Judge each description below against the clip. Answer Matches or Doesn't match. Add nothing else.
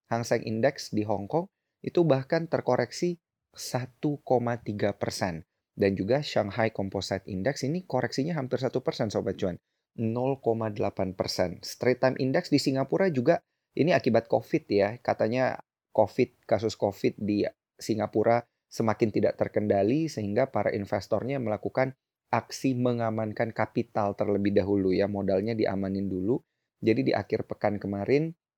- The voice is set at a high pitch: Doesn't match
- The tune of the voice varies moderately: Matches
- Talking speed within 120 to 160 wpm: Matches